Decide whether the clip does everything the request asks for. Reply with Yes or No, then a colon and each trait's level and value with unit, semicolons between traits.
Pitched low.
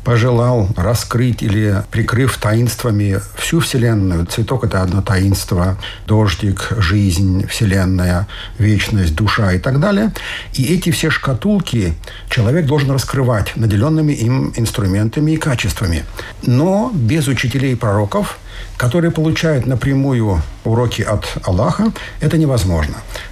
Yes: low, 115 Hz